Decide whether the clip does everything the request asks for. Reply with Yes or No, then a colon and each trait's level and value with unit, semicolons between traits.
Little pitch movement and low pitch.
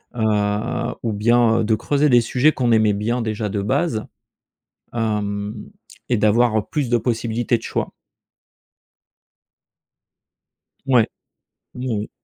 Yes: narrow, 2.3 semitones; low, 115 Hz